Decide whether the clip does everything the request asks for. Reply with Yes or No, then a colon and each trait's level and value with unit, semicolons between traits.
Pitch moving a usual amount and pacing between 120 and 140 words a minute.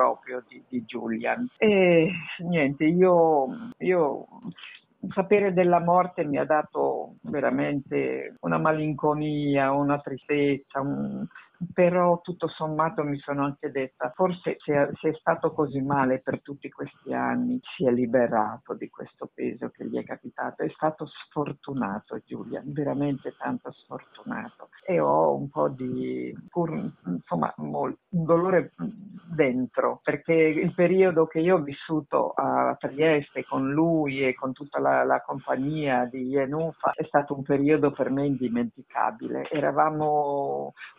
Yes: average, 3.8 semitones; average, 135 wpm